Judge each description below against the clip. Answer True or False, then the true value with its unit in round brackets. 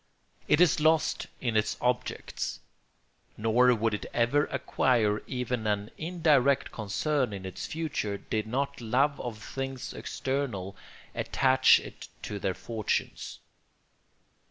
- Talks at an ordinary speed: False (120 wpm)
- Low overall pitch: True (125 Hz)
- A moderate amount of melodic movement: True (4.4 semitones)